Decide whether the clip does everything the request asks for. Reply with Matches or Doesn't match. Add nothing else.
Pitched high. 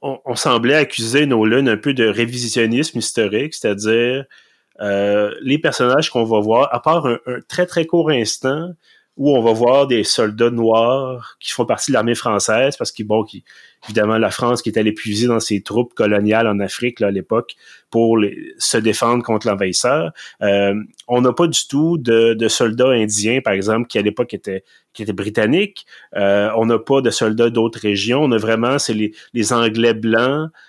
Doesn't match